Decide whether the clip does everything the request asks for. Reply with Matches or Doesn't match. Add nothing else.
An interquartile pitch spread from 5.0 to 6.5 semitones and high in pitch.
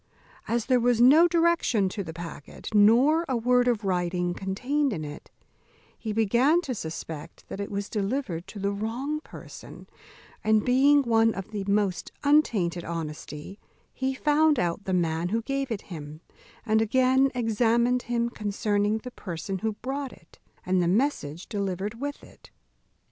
Matches